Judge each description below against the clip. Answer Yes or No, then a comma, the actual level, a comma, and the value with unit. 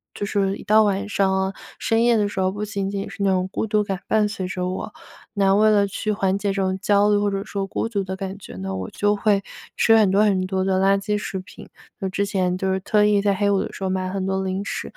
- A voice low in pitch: No, high, 195 Hz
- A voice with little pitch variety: Yes, narrow, 1.5 semitones